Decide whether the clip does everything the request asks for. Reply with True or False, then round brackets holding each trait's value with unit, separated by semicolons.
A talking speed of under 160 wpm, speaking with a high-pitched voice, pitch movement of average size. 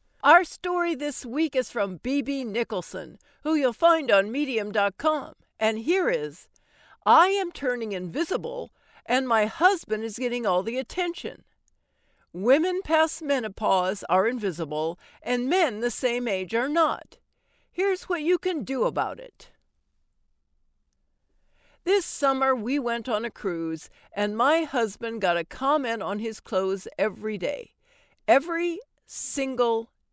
False (135 wpm; 245 Hz; 7.6 semitones)